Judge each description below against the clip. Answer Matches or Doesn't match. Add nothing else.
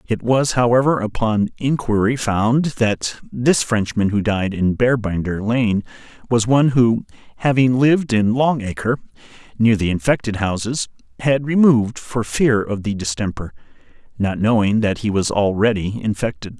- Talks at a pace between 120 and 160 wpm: Matches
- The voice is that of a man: Matches